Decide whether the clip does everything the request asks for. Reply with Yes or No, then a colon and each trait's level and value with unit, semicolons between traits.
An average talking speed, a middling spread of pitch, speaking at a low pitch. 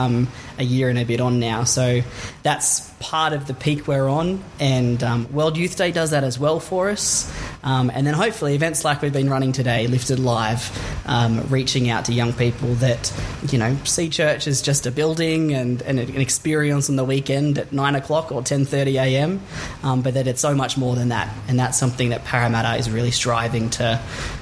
No: fast, 210 wpm; average, 3.3 semitones; low, 130 Hz